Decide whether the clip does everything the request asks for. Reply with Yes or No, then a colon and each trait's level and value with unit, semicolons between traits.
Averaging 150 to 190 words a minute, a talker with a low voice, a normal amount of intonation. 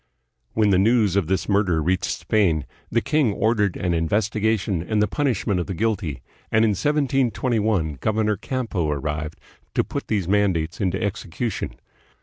Yes: average, 155 wpm; low, 100 Hz; average, 4.0 semitones